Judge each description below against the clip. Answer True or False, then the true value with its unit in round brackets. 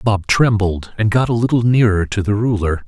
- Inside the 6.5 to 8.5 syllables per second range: False (5.1 syllables/s)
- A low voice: True (105 Hz)